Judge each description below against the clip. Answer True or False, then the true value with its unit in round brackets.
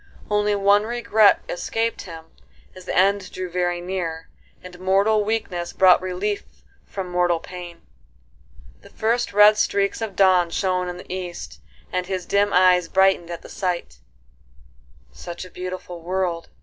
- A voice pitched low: False (185 Hz)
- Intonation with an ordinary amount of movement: False (2.2 semitones)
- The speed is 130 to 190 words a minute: True (150 wpm)